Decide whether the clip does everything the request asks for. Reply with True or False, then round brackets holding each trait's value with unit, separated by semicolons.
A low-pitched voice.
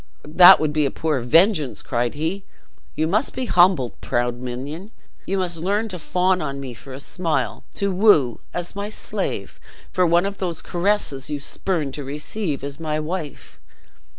False (160 Hz)